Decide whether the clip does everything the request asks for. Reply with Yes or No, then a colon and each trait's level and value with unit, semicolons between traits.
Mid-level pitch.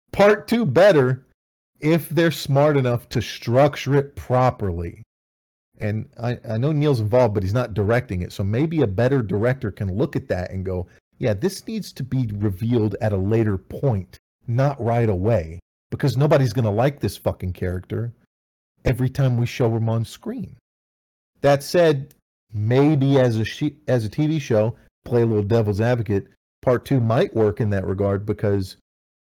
No: low, 115 Hz